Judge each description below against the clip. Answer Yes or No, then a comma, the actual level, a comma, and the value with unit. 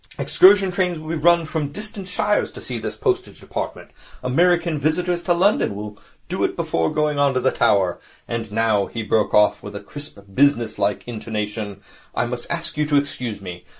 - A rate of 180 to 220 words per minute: Yes, average, 185 wpm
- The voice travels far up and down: Yes, wide, 8.2 semitones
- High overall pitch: No, medium, 140 Hz